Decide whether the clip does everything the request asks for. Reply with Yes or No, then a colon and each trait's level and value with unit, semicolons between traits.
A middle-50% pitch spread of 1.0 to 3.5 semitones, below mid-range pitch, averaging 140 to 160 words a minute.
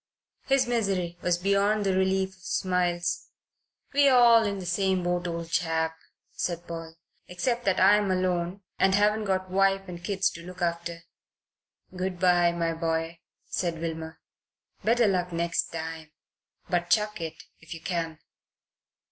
No: narrow, 2.5 semitones; medium, 180 Hz; average, 150 wpm